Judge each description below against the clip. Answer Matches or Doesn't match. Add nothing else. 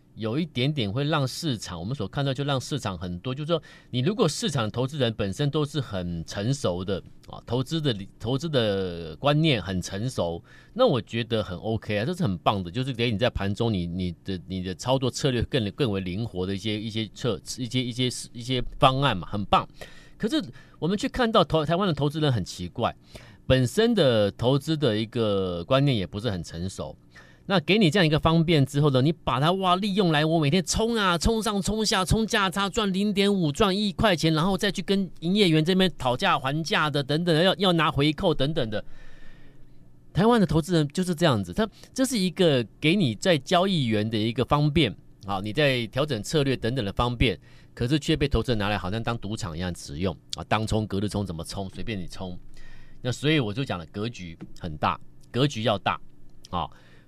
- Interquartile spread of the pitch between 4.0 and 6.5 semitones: Doesn't match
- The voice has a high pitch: Doesn't match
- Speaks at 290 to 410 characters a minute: Matches